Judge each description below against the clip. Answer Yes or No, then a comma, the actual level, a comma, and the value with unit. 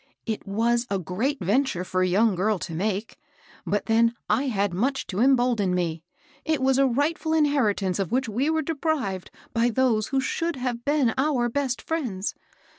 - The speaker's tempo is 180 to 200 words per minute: Yes, average, 185 wpm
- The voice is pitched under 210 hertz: No, high, 235 Hz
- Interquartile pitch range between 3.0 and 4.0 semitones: No, average, 5.3 semitones